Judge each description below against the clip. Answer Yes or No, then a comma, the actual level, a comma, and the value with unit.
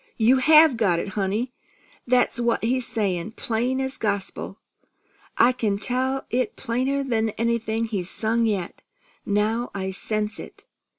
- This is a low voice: No, high, 230 Hz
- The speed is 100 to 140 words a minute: Yes, slow, 135 wpm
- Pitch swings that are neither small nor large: Yes, average, 3.3 semitones